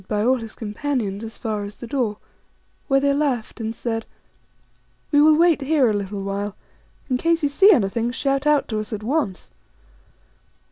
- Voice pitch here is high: Yes, high, 240 Hz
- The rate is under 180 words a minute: No, average, 185 wpm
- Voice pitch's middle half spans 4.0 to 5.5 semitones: Yes, average, 5.2 semitones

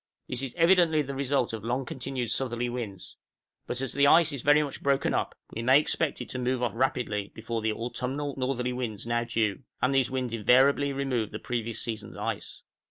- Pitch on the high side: No, low, 125 Hz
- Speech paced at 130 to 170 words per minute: No, average, 200 wpm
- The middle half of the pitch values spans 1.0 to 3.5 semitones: Yes, average, 2.9 semitones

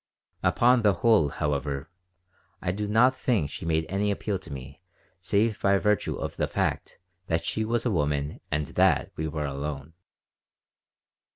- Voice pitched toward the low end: Yes, very low, 90 Hz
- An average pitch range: No, wide, 6.2 semitones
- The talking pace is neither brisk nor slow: Yes, average, 160 wpm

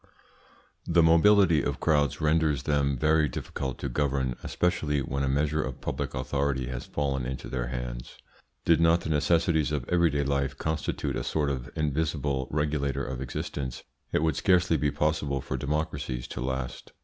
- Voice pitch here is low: Yes, very low, 70 Hz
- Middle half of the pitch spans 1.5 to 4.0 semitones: Yes, average, 2.9 semitones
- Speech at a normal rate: Yes, average, 160 wpm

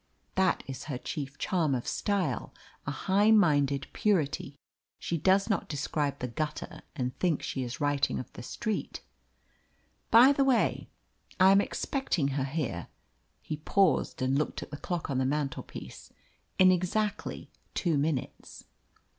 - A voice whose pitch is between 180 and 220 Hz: No, medium, 150 Hz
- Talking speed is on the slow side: No, average, 145 wpm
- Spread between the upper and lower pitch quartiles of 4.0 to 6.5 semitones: Yes, wide, 5.6 semitones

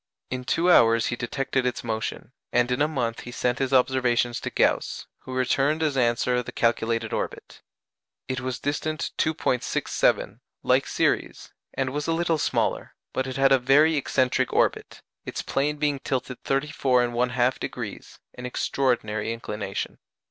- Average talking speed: Yes, average, 150 wpm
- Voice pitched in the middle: No, low, 130 Hz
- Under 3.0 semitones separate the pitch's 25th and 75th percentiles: Yes, narrow, 2.4 semitones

